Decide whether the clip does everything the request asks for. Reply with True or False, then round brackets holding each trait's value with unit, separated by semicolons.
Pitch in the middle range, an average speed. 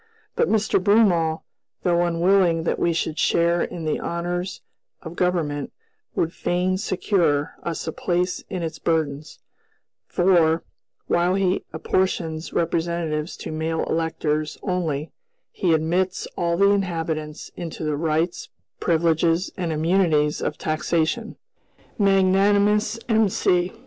False (170 Hz; 120 wpm)